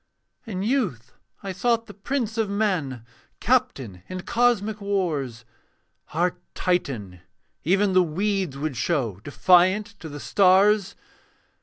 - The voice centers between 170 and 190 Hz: Yes, medium, 185 Hz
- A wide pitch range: Yes, wide, 6.4 semitones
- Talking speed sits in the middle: No, slow, 120 wpm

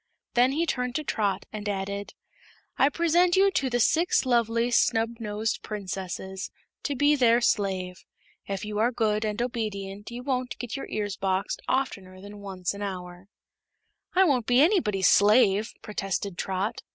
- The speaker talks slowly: No, average, 155 wpm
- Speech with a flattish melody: No, average, 4.2 semitones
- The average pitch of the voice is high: Yes, high, 215 Hz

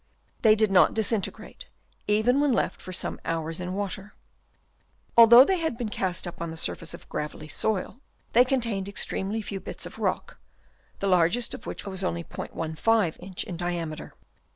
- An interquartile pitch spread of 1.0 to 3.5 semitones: No, average, 4.4 semitones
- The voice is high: Yes, high, 195 Hz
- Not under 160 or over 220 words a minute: Yes, average, 170 wpm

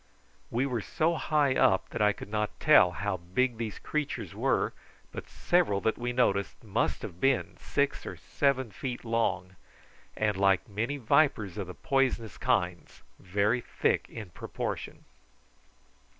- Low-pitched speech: Yes, low, 115 Hz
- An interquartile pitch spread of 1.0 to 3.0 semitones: No, average, 5.3 semitones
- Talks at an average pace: Yes, average, 150 wpm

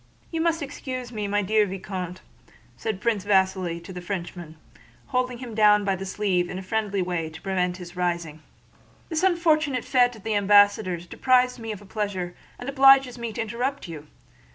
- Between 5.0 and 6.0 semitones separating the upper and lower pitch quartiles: Yes, wide, 5.4 semitones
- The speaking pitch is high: Yes, high, 205 Hz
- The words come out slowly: No, average, 175 wpm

